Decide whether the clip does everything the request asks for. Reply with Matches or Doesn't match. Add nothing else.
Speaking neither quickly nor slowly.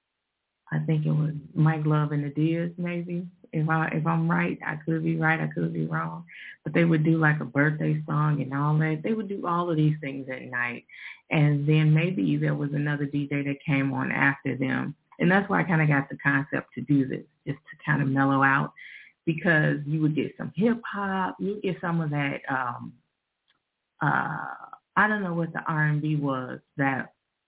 Doesn't match